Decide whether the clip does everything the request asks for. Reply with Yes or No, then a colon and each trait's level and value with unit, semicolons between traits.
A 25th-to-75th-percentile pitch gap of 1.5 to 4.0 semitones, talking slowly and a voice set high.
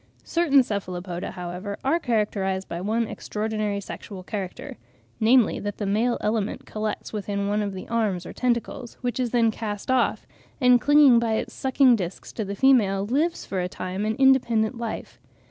No: average, 3.6 semitones; average, 170 wpm; high, 215 Hz